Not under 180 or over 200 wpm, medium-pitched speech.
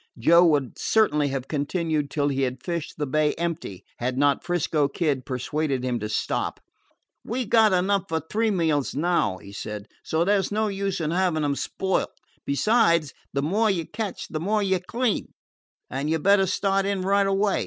Yes: average, 190 wpm; medium, 165 Hz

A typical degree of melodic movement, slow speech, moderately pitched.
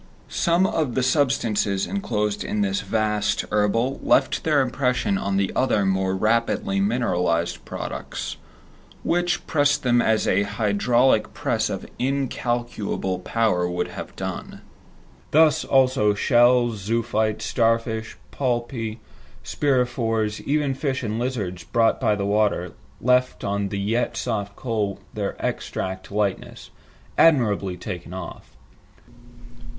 No: average, 4.2 semitones; slow, 120 wpm; low, 115 Hz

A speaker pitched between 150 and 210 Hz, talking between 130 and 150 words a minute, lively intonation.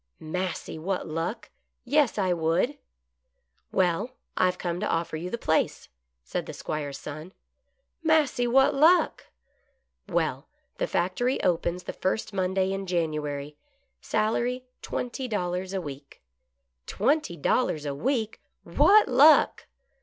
Yes: medium, 185 Hz; average, 140 wpm; wide, 7.1 semitones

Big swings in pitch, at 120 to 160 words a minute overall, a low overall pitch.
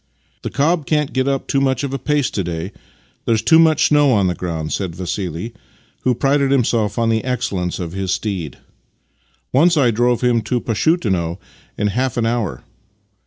No: wide, 6.3 semitones; average, 185 wpm; low, 115 Hz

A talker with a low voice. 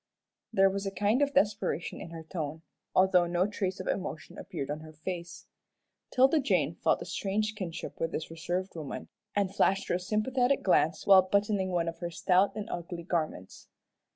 No: medium, 185 Hz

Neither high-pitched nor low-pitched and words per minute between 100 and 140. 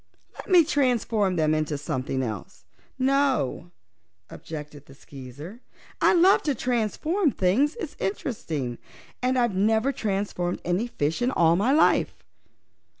No: high, 205 Hz; slow, 135 wpm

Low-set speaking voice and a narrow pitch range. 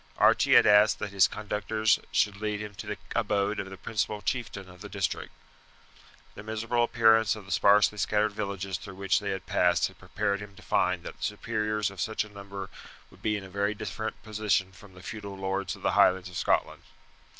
Yes: low, 100 Hz; narrow, 1.8 semitones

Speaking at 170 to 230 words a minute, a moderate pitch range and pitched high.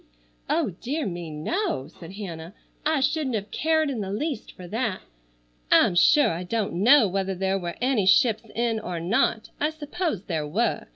No: average, 175 wpm; wide, 7.4 semitones; high, 215 Hz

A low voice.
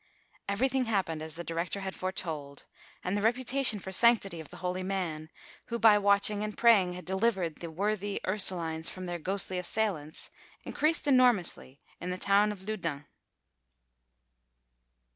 No: high, 190 Hz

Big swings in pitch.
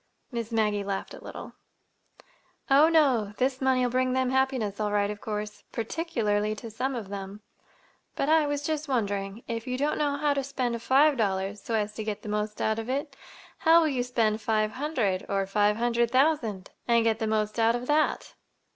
No: average, 4.1 semitones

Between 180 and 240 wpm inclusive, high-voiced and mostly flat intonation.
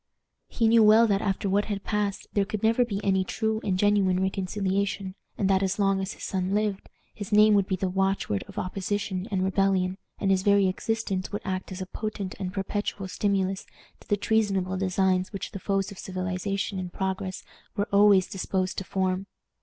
Yes: average, 195 wpm; high, 195 Hz; narrow, 1.4 semitones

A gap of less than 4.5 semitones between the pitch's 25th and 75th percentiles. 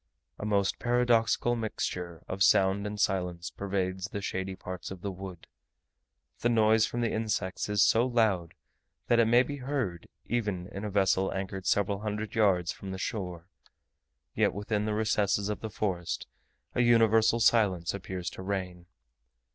Yes: average, 3.0 semitones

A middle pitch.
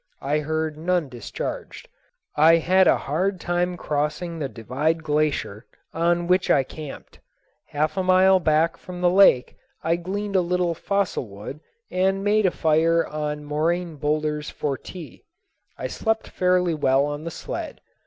Yes: medium, 165 Hz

